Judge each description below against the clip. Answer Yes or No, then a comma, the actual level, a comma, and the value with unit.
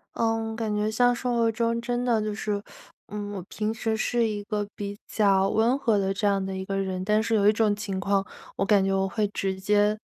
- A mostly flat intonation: Yes, narrow, 2.2 semitones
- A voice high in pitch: Yes, high, 210 Hz